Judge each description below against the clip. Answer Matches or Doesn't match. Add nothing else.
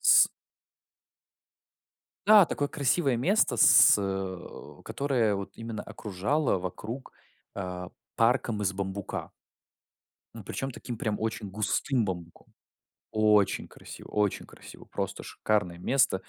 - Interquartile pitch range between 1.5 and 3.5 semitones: Doesn't match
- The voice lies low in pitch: Matches